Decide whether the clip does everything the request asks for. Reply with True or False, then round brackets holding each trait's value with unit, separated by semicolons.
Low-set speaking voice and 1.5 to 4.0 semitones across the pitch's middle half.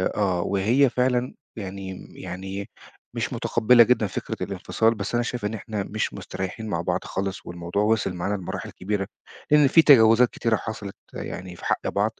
True (105 Hz; 3.6 semitones)